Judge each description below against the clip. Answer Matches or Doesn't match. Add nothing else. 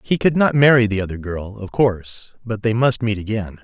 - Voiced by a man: Matches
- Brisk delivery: Matches